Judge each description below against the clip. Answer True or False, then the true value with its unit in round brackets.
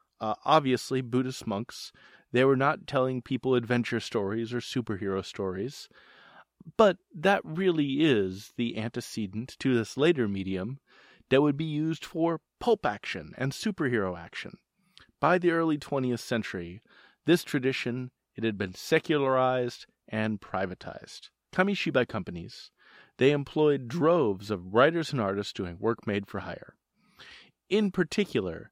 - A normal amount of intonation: False (6.0 semitones)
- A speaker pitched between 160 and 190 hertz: False (130 Hz)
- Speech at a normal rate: False (125 wpm)